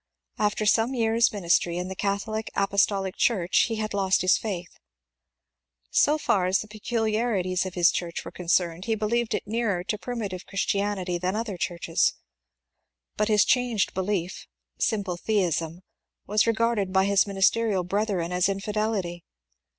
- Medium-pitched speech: No, high, 200 Hz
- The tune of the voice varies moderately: Yes, average, 3.1 semitones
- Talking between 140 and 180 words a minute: Yes, average, 150 wpm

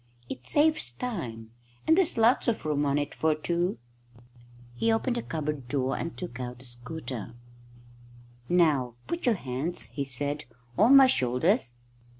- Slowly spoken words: No, average, 155 wpm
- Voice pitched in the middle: Yes, medium, 150 Hz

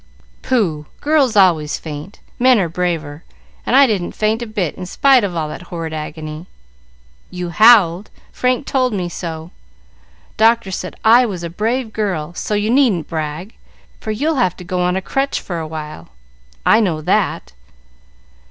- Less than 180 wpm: Yes, average, 165 wpm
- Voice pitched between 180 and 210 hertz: Yes, medium, 185 Hz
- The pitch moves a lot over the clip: Yes, wide, 5.8 semitones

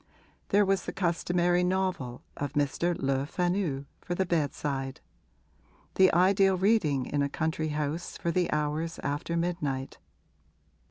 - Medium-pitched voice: Yes, medium, 165 Hz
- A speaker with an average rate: No, slow, 130 wpm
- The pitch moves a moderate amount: Yes, average, 3.9 semitones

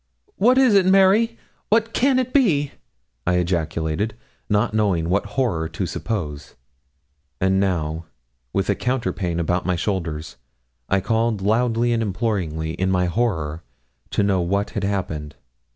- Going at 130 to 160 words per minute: Yes, average, 140 wpm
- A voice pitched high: No, low, 100 Hz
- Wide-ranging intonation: Yes, wide, 5.9 semitones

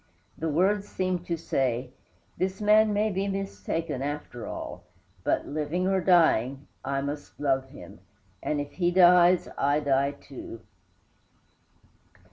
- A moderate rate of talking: No, slow, 130 wpm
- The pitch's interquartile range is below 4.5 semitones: No, average, 4.9 semitones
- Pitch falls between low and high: Yes, medium, 160 Hz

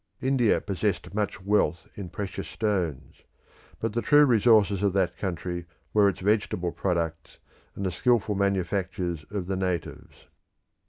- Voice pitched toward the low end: Yes, low, 100 Hz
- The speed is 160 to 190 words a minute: No, average, 140 wpm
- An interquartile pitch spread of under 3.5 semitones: Yes, average, 2.9 semitones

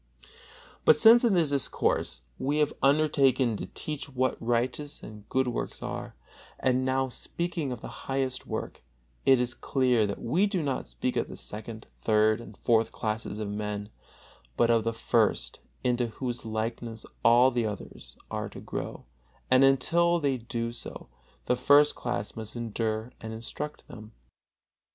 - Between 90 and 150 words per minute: No, average, 160 wpm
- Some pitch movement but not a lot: Yes, average, 3.4 semitones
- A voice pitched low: Yes, low, 125 Hz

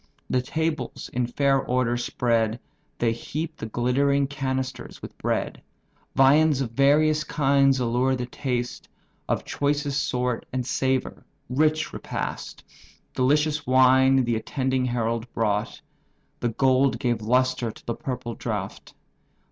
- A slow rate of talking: Yes, slow, 125 wpm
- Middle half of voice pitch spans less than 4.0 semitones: Yes, narrow, 2.4 semitones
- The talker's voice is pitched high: No, low, 130 Hz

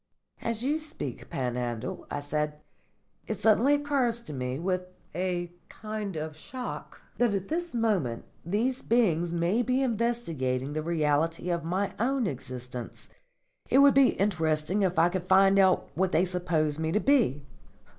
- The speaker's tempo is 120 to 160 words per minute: Yes, average, 155 wpm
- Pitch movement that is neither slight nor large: No, wide, 7.1 semitones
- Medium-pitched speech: Yes, medium, 180 Hz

